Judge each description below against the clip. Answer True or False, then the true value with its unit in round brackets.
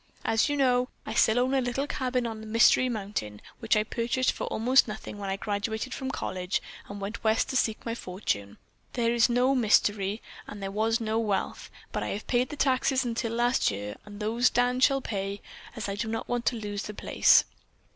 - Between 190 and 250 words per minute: True (205 wpm)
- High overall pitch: True (225 Hz)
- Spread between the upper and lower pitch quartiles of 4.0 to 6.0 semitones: False (3.2 semitones)